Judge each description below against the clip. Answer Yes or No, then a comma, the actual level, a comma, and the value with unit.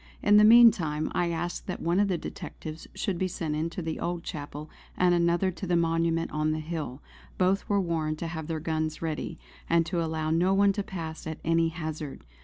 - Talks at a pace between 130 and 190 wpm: No, fast, 205 wpm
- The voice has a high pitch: No, medium, 165 Hz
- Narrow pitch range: Yes, narrow, 2.2 semitones